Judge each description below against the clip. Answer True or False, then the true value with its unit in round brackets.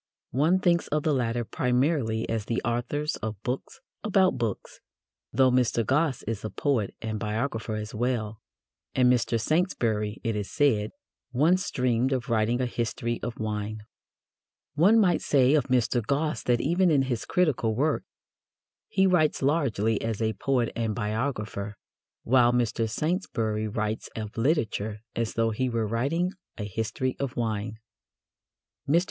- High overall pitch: False (120 Hz)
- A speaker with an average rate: True (150 wpm)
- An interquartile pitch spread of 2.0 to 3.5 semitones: False (4.4 semitones)